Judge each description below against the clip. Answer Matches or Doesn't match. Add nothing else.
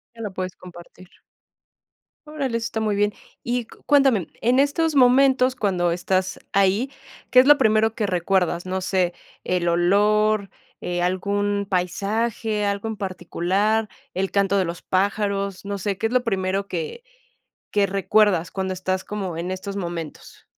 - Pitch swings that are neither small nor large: Matches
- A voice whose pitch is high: Matches